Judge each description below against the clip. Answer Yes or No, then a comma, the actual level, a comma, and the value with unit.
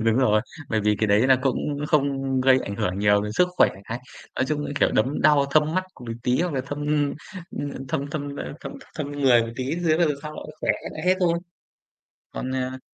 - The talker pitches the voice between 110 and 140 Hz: Yes, low, 135 Hz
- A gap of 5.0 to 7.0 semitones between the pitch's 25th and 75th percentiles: No, average, 4.0 semitones